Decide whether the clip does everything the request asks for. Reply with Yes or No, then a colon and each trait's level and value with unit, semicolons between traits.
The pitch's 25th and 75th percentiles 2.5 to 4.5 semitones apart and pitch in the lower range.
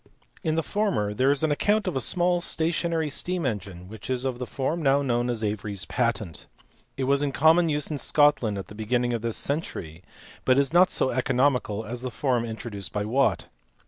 No: wide, 5.4 semitones; low, 130 Hz